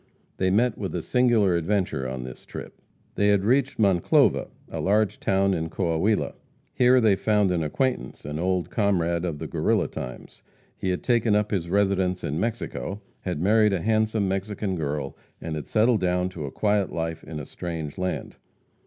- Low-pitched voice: Yes, very low, 95 Hz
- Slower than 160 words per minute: No, average, 180 wpm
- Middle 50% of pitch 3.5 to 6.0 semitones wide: Yes, average, 4.0 semitones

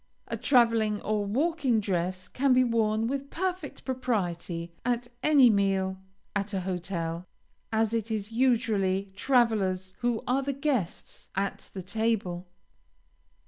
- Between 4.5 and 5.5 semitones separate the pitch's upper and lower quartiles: Yes, average, 4.8 semitones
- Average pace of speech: No, slow, 130 wpm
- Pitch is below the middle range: No, high, 220 Hz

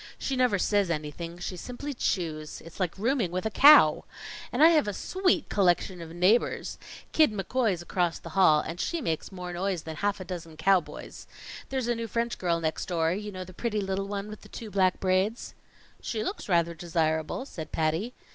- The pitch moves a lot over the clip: No, average, 4.6 semitones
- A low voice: No, high, 190 Hz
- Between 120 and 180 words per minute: No, average, 195 wpm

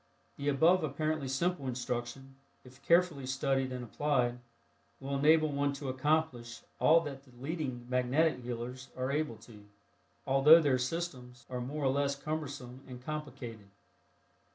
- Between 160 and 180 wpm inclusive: No, average, 140 wpm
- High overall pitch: No, low, 135 Hz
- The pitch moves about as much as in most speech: Yes, average, 3.3 semitones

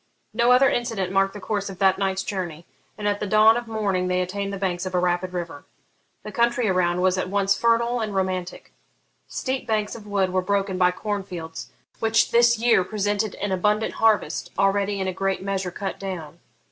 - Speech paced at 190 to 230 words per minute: Yes, average, 200 wpm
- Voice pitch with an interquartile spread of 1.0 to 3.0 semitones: Yes, narrow, 2.6 semitones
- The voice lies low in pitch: No, high, 195 Hz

